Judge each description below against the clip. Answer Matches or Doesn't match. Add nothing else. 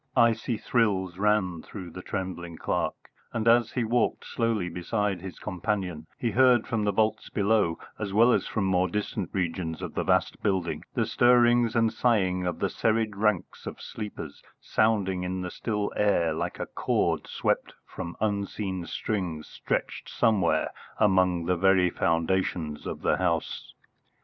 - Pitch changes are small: Doesn't match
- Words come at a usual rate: Matches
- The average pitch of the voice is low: Matches